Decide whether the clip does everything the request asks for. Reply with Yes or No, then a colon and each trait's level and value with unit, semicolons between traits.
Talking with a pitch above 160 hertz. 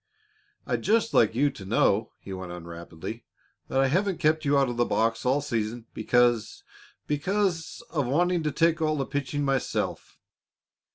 No: low, 135 Hz